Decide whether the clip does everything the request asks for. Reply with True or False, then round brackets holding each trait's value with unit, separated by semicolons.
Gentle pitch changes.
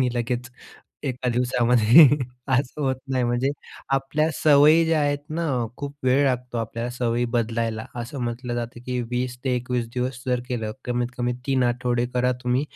True (1.6 semitones)